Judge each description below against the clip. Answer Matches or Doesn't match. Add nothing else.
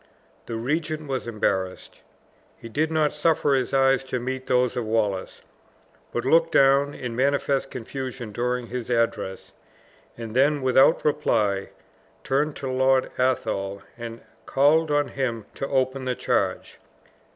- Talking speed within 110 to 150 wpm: Matches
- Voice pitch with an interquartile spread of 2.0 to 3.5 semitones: Matches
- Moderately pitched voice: Doesn't match